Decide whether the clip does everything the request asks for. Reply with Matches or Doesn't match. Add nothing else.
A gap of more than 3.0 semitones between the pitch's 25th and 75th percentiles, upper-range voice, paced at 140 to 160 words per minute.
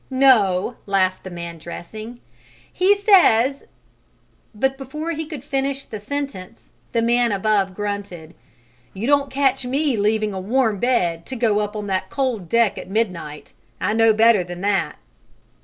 Matches